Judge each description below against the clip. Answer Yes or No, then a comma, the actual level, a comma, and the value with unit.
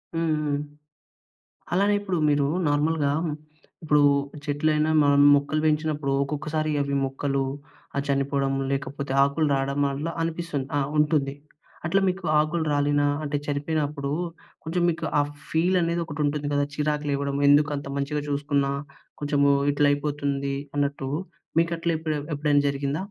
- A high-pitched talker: No, medium, 145 Hz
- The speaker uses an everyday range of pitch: No, narrow, 1.7 semitones